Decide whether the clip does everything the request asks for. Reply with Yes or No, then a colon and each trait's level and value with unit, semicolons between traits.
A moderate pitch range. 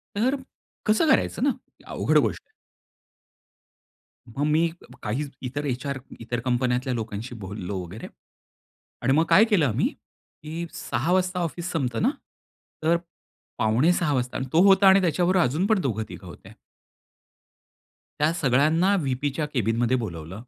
No: wide, 6.3 semitones